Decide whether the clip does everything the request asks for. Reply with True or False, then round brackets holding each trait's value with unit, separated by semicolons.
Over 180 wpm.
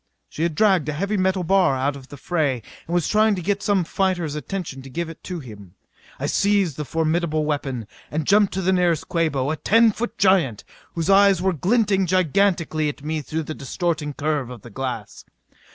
True (200 wpm)